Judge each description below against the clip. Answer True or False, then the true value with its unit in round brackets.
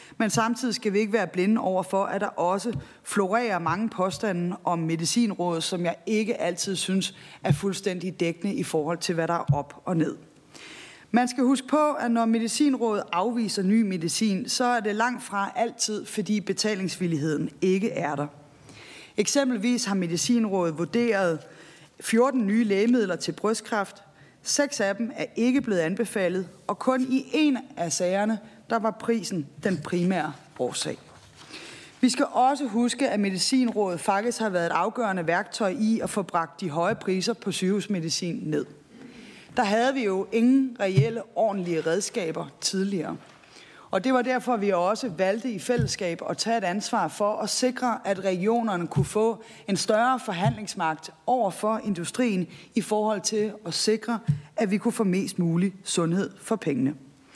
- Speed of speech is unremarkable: True (160 wpm)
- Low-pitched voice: False (205 Hz)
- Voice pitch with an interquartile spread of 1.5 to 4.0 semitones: False (4.5 semitones)